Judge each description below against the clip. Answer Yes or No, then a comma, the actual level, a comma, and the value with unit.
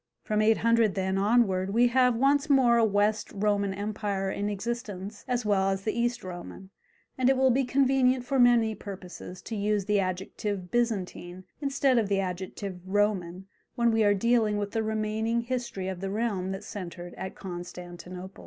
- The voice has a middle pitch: No, high, 210 Hz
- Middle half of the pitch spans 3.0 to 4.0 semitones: Yes, average, 3.7 semitones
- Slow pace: No, average, 170 wpm